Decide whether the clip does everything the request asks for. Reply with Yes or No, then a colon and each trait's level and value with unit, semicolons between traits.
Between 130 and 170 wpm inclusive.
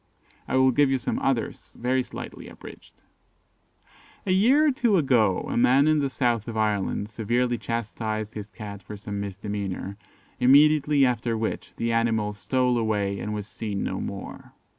Yes: average, 160 wpm